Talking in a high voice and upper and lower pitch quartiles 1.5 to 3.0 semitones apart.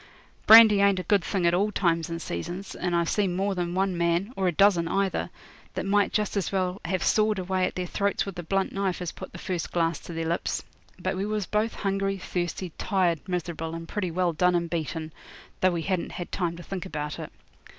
No: medium, 180 Hz; narrow, 2.5 semitones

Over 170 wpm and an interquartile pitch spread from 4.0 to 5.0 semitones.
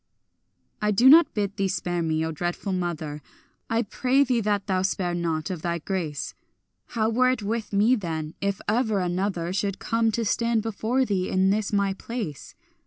Yes: average, 180 wpm; average, 4.4 semitones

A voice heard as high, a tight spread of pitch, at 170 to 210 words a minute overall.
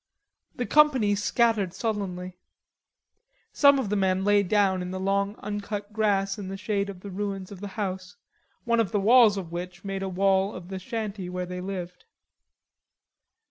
Yes: high, 195 Hz; narrow, 1.9 semitones; average, 175 wpm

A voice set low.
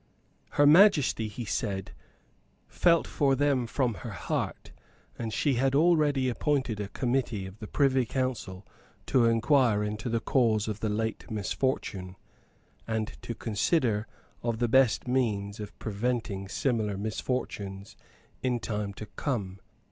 Yes: low, 115 Hz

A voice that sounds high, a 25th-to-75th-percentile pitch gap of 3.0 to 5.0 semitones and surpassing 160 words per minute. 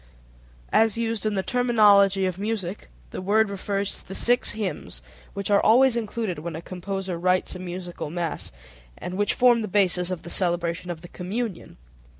Yes: high, 195 Hz; average, 3.4 semitones; average, 175 wpm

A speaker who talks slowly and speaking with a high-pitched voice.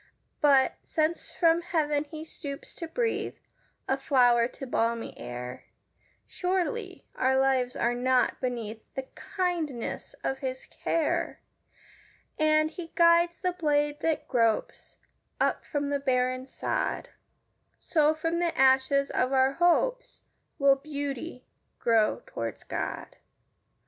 Yes: slow, 125 wpm; very high, 285 Hz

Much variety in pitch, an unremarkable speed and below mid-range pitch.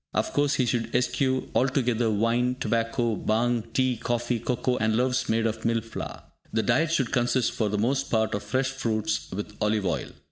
No: narrow, 2.5 semitones; average, 185 wpm; low, 120 Hz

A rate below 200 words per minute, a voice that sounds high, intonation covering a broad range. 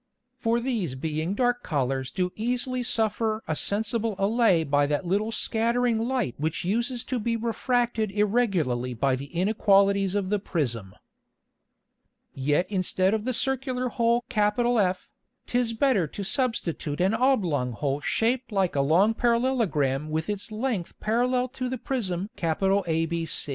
Yes: average, 140 wpm; high, 205 Hz; wide, 6.4 semitones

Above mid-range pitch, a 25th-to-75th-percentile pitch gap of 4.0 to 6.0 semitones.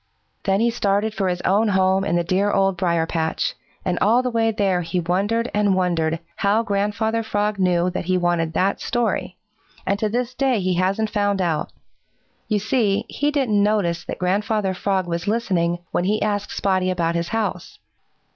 No: high, 195 Hz; average, 3.0 semitones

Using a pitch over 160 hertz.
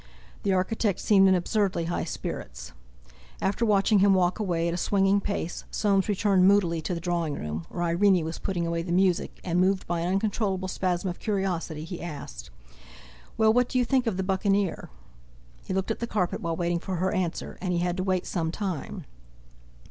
Yes: medium, 185 Hz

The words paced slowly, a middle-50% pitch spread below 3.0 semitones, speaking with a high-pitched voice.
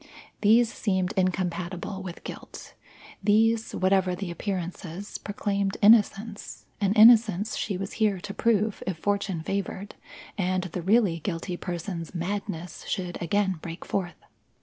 Yes: slow, 125 wpm; narrow, 2.5 semitones; high, 195 Hz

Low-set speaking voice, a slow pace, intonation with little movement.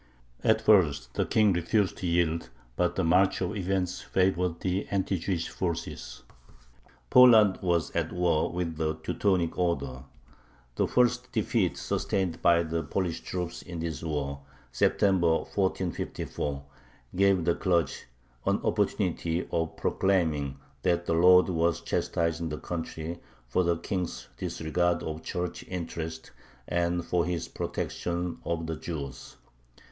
Yes: very low, 85 Hz; slow, 130 wpm; narrow, 2.1 semitones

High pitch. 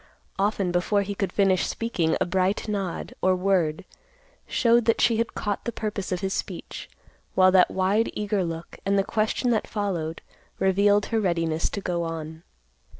Yes: high, 195 Hz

